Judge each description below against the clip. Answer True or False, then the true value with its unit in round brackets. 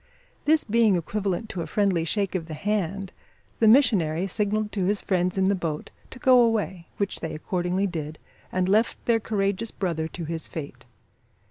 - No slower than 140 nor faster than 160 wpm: False (175 wpm)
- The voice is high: True (195 Hz)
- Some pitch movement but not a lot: True (3.8 semitones)